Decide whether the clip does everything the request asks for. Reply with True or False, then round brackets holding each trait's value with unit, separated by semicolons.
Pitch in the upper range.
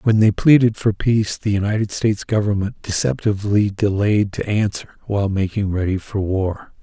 False (105 Hz)